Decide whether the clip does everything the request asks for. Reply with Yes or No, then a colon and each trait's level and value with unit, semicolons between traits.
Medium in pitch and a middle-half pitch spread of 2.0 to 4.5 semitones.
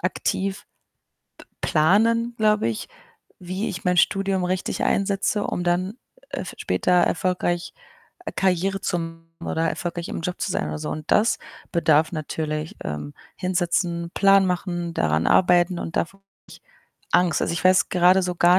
Yes: medium, 180 Hz; narrow, 2.4 semitones